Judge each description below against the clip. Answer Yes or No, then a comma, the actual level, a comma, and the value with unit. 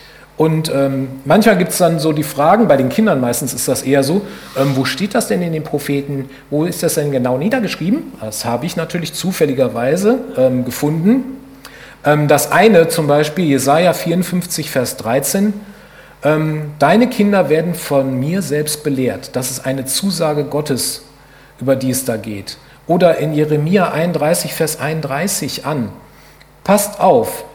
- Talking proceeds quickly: No, average, 160 wpm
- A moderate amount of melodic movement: Yes, average, 4.5 semitones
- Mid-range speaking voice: Yes, medium, 150 Hz